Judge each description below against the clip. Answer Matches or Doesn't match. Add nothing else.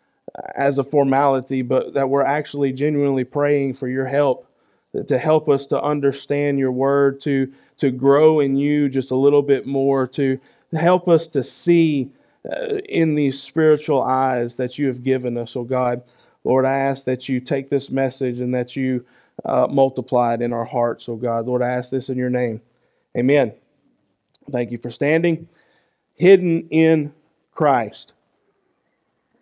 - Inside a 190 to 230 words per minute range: Doesn't match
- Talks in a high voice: Doesn't match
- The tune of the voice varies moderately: Doesn't match